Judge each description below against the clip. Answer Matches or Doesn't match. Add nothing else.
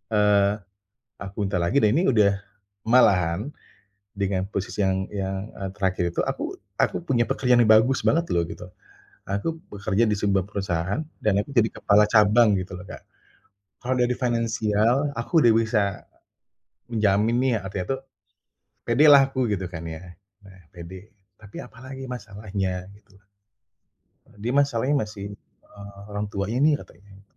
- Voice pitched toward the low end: Matches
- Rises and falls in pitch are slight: Doesn't match